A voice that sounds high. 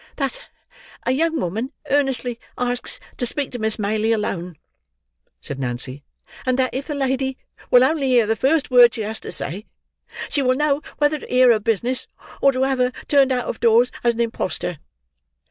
Yes: very high, 250 Hz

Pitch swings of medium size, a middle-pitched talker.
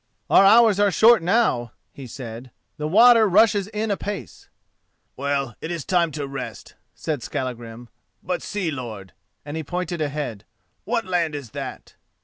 No: wide, 7.8 semitones; medium, 160 Hz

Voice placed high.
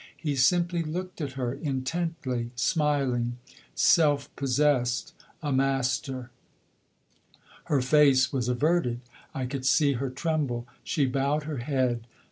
No: low, 135 Hz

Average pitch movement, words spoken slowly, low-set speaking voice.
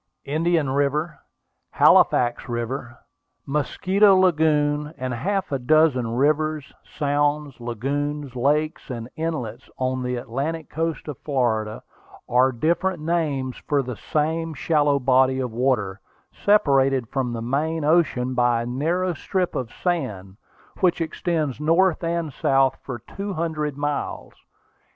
No: average, 4.1 semitones; slow, 125 wpm; medium, 145 Hz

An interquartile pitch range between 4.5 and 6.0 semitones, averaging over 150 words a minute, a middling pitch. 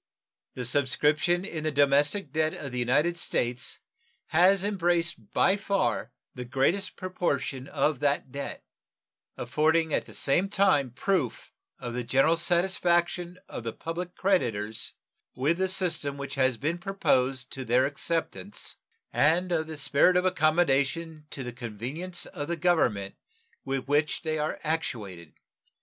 No: average, 4.8 semitones; average, 140 wpm; medium, 155 Hz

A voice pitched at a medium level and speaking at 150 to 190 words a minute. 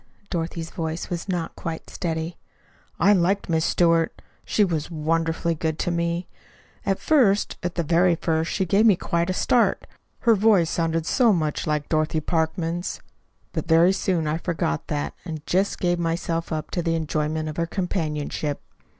Yes: medium, 165 Hz; average, 165 wpm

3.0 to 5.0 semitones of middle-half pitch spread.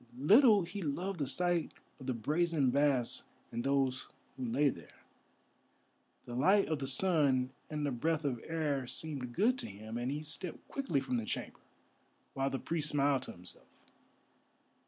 Yes: average, 4.3 semitones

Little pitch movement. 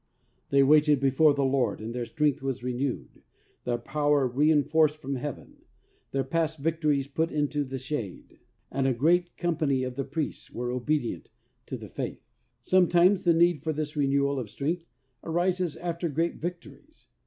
No: average, 3.4 semitones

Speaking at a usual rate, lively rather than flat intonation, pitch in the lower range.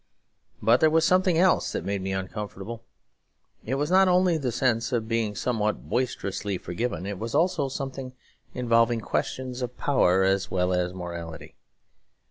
Yes: average, 155 wpm; wide, 5.8 semitones; low, 115 Hz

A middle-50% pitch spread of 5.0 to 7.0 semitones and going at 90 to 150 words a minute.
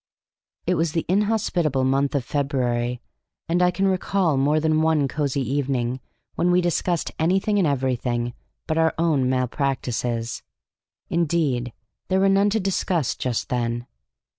Yes: wide, 5.4 semitones; average, 140 wpm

